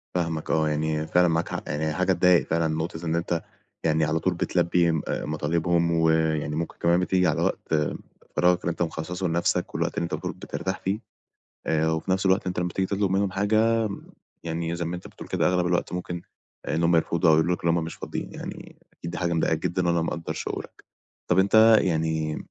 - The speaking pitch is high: No, very low, 85 Hz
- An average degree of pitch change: No, narrow, 2.0 semitones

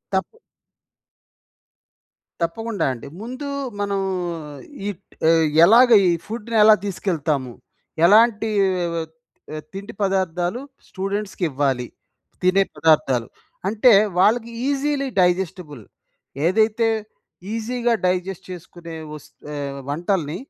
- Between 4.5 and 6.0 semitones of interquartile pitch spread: Yes, average, 5.1 semitones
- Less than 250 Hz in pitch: Yes, high, 190 Hz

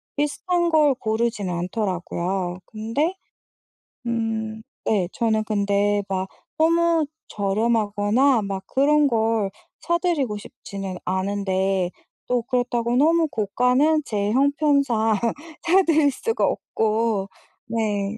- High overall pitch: Yes, high, 225 Hz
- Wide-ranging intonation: Yes, wide, 5.7 semitones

